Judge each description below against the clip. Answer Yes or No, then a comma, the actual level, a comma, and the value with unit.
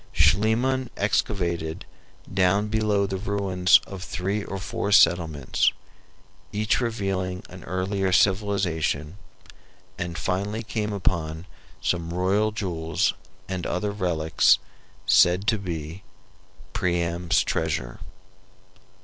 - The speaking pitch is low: Yes, very low, 95 Hz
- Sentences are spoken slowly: Yes, slow, 100 wpm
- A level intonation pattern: No, average, 3.0 semitones